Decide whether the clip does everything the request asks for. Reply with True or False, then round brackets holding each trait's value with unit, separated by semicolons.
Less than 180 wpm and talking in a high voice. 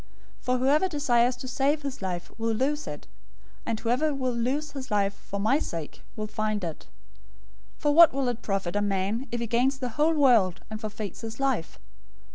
False (200 wpm; 240 Hz)